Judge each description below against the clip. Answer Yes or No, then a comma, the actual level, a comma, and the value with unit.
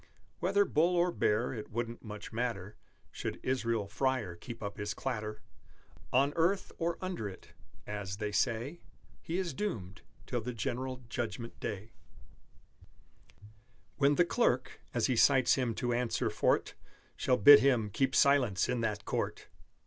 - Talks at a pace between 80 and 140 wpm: No, average, 150 wpm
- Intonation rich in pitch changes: No, average, 4.6 semitones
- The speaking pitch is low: Yes, low, 120 Hz